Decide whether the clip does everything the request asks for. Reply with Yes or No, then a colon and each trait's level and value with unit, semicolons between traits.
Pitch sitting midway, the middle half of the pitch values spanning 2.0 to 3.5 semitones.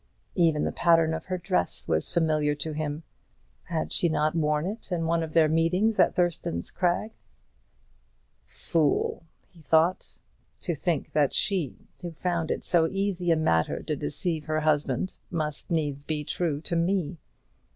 Yes: medium, 165 Hz; narrow, 2.4 semitones